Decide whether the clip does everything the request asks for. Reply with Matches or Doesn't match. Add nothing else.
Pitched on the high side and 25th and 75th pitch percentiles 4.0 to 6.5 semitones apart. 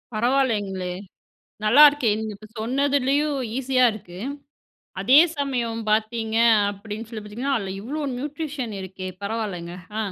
Matches